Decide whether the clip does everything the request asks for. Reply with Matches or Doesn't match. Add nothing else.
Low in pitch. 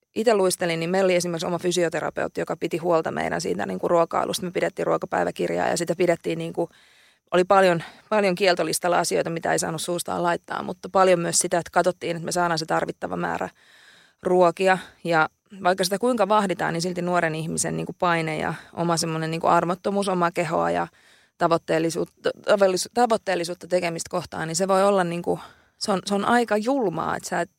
Doesn't match